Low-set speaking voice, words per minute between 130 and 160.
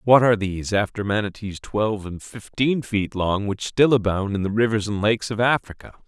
No: low, 105 Hz; average, 195 wpm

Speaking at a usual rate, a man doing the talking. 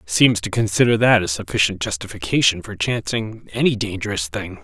Yes: average, 155 wpm; male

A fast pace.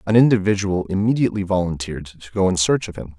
No: average, 190 wpm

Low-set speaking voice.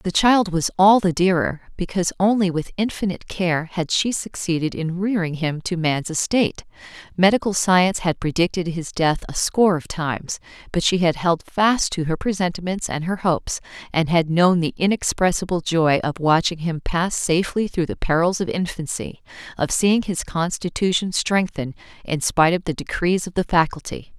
No: medium, 175 Hz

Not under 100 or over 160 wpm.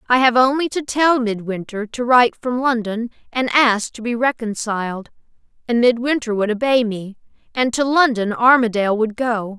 Yes: average, 155 wpm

